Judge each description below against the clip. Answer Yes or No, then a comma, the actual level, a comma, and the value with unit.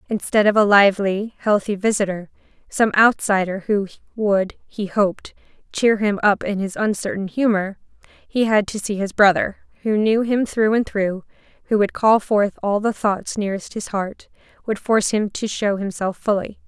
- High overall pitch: Yes, high, 205 Hz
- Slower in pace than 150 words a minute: No, average, 175 wpm